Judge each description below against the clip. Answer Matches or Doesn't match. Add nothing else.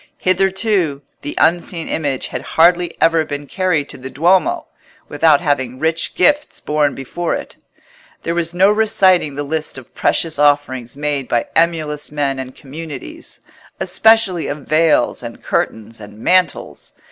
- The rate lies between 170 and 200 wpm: Doesn't match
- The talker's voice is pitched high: Doesn't match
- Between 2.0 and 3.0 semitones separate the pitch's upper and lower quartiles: Doesn't match